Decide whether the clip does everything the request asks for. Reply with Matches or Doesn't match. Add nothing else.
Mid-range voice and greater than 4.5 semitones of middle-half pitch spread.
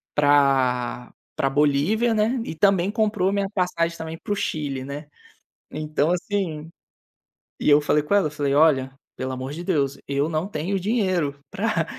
Matches